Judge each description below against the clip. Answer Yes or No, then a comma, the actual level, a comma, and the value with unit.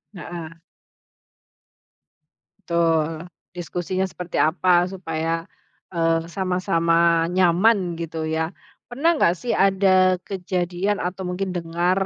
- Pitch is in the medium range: Yes, medium, 175 Hz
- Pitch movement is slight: Yes, narrow, 2.1 semitones